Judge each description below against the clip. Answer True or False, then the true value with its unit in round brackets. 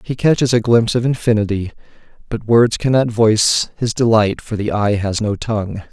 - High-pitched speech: False (110 Hz)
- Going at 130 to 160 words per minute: False (180 wpm)